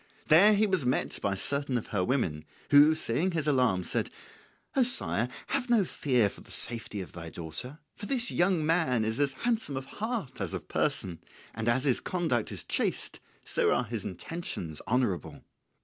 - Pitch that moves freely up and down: Yes, wide, 8.1 semitones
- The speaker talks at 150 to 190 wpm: Yes, average, 185 wpm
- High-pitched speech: No, low, 130 Hz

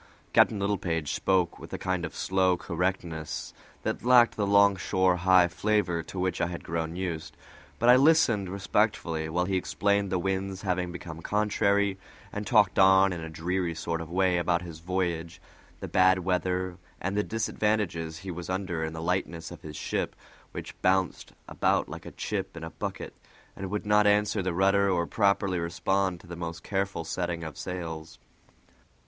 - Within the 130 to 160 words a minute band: No, average, 175 wpm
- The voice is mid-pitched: No, very low, 95 Hz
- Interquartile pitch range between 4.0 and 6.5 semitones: No, narrow, 2.6 semitones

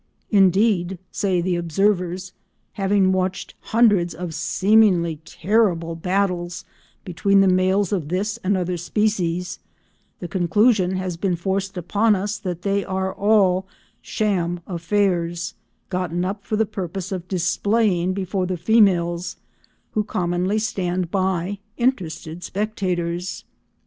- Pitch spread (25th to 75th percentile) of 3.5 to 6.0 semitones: No, narrow, 2.4 semitones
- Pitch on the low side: No, medium, 185 Hz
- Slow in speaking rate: Yes, slow, 120 wpm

